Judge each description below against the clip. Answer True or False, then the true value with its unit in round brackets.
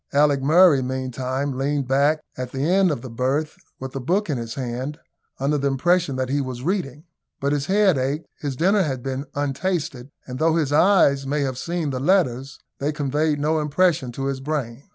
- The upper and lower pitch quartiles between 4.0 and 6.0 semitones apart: False (3.0 semitones)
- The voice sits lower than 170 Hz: True (140 Hz)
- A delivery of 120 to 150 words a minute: False (195 wpm)